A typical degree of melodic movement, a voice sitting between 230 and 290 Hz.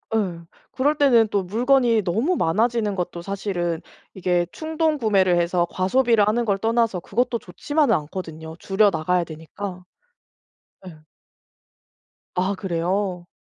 No: average, 4.8 semitones; high, 195 Hz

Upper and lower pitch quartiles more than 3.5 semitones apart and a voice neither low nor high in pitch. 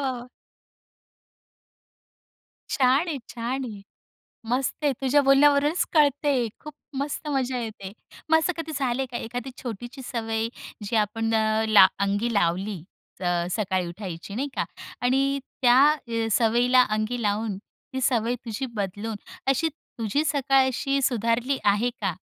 No: average, 3.9 semitones; high, 240 Hz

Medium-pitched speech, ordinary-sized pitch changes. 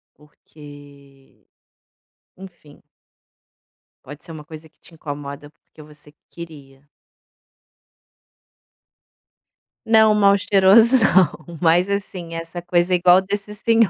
Yes: medium, 170 Hz; average, 4.6 semitones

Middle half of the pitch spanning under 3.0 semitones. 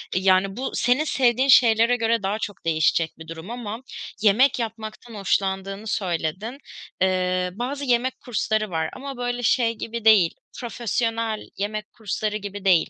No: average, 3.9 semitones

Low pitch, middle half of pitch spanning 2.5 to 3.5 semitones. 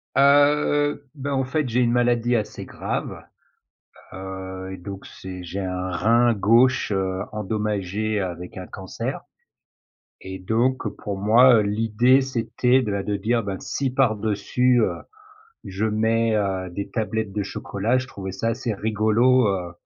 No: low, 110 Hz; average, 4.0 semitones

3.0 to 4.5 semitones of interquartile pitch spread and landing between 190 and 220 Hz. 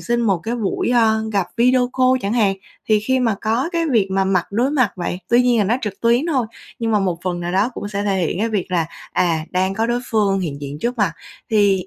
Yes: average, 4.0 semitones; high, 210 Hz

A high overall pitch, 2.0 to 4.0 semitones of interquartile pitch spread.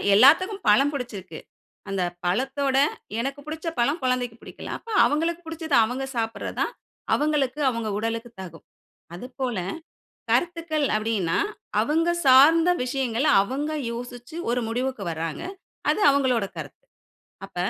No: very high, 260 Hz; average, 4.9 semitones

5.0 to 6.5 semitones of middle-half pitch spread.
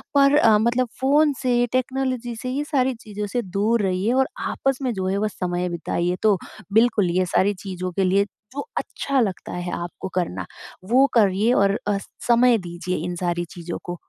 Yes: wide, 5.6 semitones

